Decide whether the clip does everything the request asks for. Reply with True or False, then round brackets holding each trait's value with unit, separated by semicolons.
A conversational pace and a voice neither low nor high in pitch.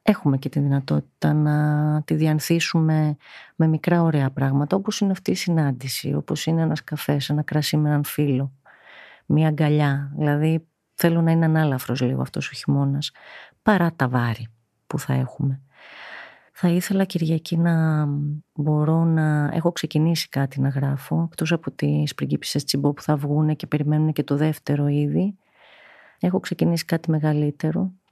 True (150 wpm; 150 Hz)